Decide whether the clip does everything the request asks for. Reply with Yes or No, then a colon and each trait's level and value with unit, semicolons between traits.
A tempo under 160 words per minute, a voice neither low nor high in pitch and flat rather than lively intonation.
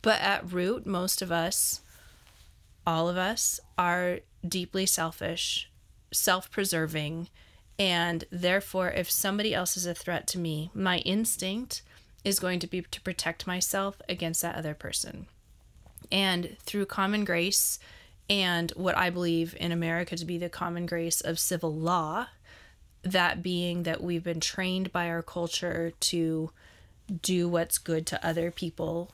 Yes: average, 145 wpm; medium, 175 Hz; narrow, 1.7 semitones